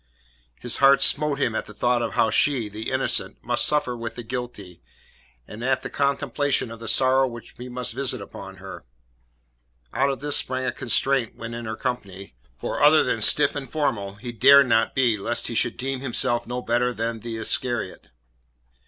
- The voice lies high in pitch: No, low, 120 Hz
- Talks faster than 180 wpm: Yes, average, 190 wpm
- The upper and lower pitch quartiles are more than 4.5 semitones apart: No, average, 2.9 semitones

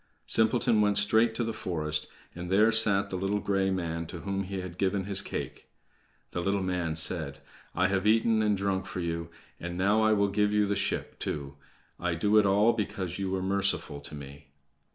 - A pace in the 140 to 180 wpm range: No, average, 200 wpm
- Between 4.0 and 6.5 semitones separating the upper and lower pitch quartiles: No, average, 2.9 semitones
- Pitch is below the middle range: Yes, very low, 95 Hz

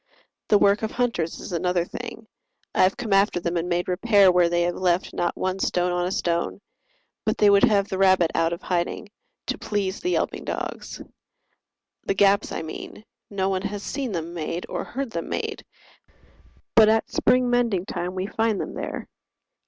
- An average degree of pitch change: Yes, average, 3.0 semitones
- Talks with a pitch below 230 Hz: Yes, high, 190 Hz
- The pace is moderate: Yes, average, 190 wpm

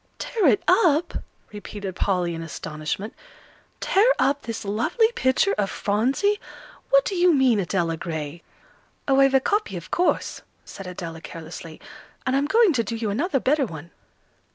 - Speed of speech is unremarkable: Yes, average, 155 wpm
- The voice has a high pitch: Yes, high, 235 Hz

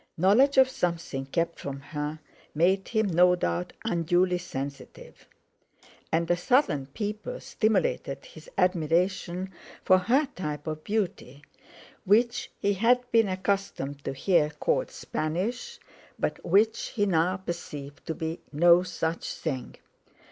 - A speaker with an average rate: No, slow, 125 wpm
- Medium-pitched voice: Yes, medium, 180 Hz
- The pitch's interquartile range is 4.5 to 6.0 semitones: Yes, average, 4.8 semitones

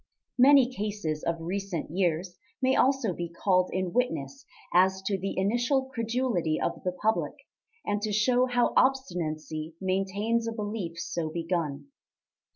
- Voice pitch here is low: No, high, 195 Hz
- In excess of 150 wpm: No, average, 140 wpm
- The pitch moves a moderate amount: No, wide, 5.9 semitones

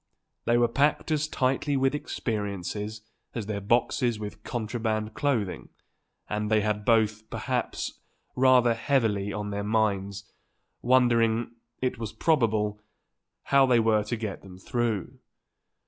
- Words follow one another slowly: Yes, slow, 130 wpm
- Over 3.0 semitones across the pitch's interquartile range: No, average, 2.7 semitones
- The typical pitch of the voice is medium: No, low, 110 Hz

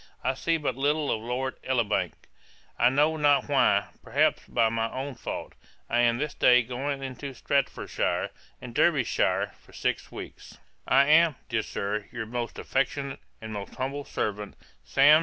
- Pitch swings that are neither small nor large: Yes, average, 3.4 semitones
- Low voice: Yes, low, 130 Hz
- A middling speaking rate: Yes, average, 160 wpm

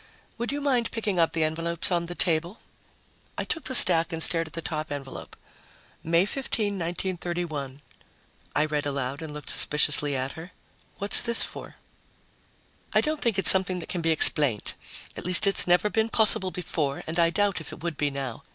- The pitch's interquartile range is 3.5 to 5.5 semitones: Yes, average, 4.3 semitones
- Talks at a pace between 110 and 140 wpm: No, average, 190 wpm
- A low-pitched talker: No, medium, 170 Hz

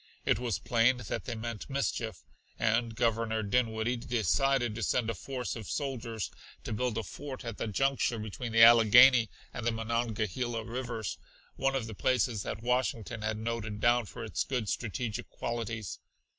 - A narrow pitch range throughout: Yes, narrow, 1.9 semitones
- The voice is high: No, low, 115 Hz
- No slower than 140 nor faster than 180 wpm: Yes, average, 165 wpm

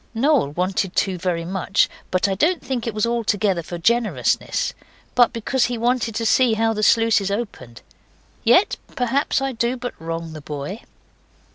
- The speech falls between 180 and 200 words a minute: No, average, 165 wpm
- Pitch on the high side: Yes, high, 220 Hz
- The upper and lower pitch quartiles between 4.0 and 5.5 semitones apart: Yes, average, 4.7 semitones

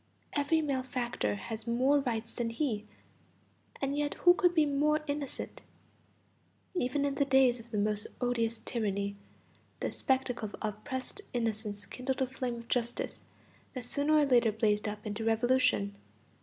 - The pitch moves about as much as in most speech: Yes, average, 4.1 semitones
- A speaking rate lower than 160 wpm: Yes, average, 150 wpm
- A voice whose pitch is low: No, high, 245 Hz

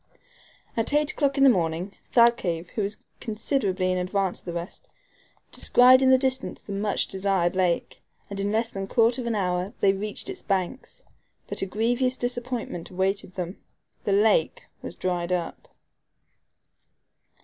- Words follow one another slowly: No, average, 160 wpm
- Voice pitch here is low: No, high, 200 Hz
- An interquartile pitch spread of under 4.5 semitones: No, average, 4.8 semitones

